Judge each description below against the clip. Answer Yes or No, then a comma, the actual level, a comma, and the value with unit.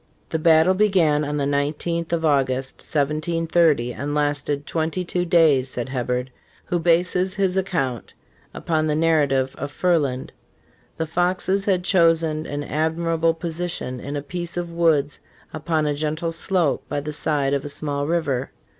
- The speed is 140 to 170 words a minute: Yes, average, 155 wpm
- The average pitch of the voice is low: No, medium, 155 Hz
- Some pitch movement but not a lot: Yes, average, 3.0 semitones